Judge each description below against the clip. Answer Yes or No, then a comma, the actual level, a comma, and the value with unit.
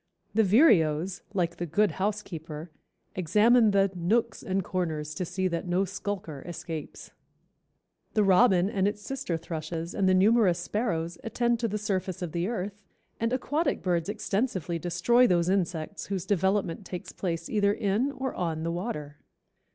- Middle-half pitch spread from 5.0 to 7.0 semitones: No, average, 3.7 semitones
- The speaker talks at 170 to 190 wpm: No, average, 155 wpm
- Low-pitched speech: No, medium, 185 Hz